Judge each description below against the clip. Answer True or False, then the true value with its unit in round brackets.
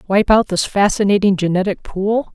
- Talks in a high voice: True (200 Hz)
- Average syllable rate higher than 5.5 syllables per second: False (5.2 syllables/s)